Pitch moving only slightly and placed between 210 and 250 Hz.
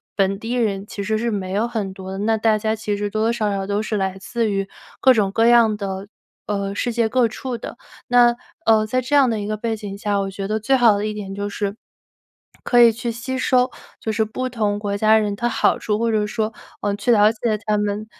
Yes: narrow, 2.3 semitones; high, 215 Hz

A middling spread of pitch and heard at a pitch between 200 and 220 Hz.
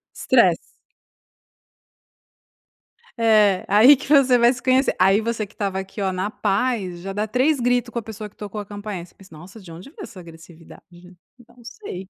Yes: average, 4.3 semitones; high, 210 Hz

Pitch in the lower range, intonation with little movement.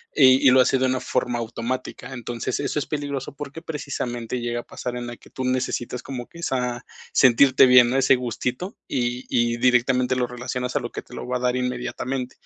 Yes: low, 125 Hz; narrow, 1.4 semitones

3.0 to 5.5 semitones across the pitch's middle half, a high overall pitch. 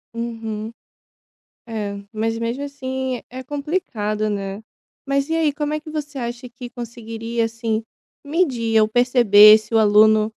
Yes: average, 3.3 semitones; high, 230 Hz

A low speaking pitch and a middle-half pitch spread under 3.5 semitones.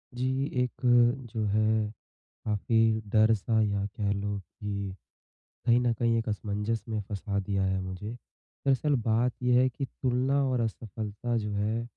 Yes: low, 110 Hz; average, 2.8 semitones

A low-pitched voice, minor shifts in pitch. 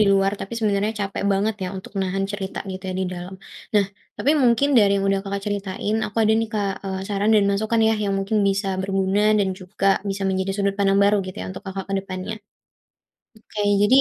No: high, 195 Hz; narrow, 1.4 semitones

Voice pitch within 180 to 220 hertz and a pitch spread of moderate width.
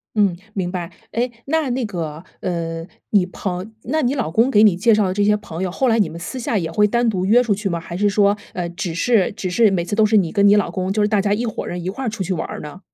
Yes: high, 200 Hz; average, 3.6 semitones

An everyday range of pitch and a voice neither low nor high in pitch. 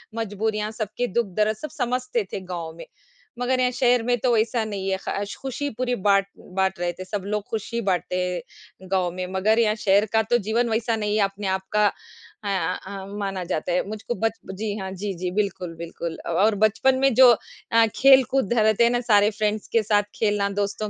No: average, 3.3 semitones; high, 210 Hz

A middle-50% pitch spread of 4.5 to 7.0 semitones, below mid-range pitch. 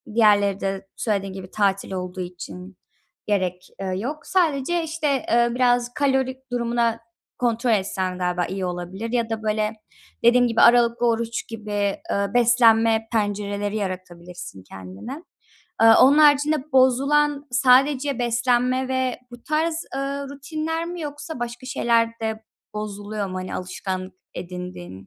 No: average, 5.0 semitones; high, 230 Hz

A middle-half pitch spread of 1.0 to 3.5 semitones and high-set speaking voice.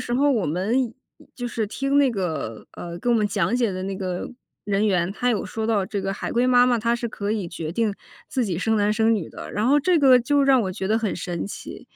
No: average, 4.3 semitones; high, 220 Hz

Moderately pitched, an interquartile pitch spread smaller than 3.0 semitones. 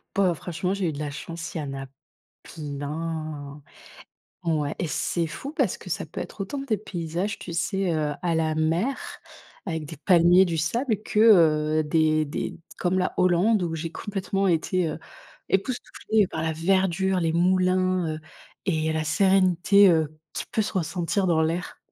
No: medium, 170 Hz; average, 3.3 semitones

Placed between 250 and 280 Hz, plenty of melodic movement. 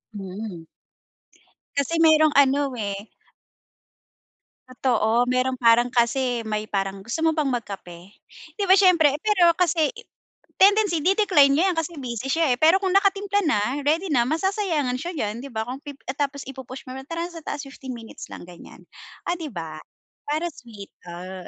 Yes: very high, 270 Hz; wide, 6.2 semitones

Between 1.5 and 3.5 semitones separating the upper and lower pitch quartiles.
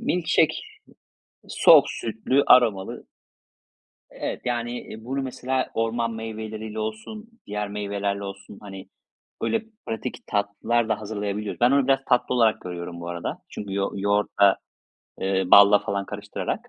Yes: average, 3.0 semitones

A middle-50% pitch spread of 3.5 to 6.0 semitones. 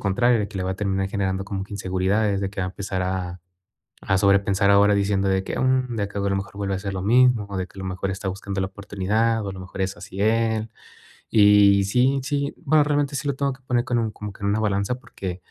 No: average, 2.8 semitones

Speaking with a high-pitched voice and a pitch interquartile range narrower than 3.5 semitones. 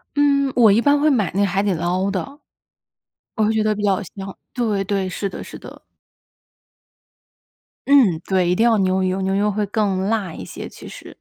Yes: high, 200 Hz; average, 2.8 semitones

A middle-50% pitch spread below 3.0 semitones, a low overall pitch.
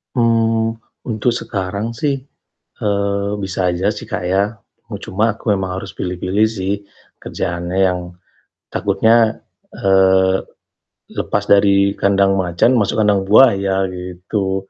Yes: narrow, 2.6 semitones; low, 100 Hz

